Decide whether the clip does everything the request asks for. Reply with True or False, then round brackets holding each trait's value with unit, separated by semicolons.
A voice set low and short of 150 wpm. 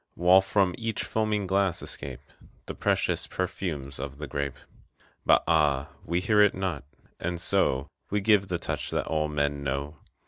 False (85 Hz; 165 wpm)